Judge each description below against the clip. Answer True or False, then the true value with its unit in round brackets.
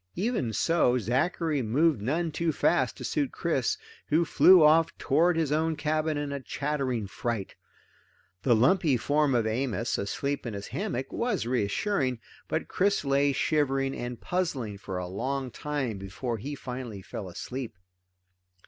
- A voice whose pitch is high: False (135 Hz)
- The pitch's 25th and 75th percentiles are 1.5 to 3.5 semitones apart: False (5.0 semitones)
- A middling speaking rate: True (150 wpm)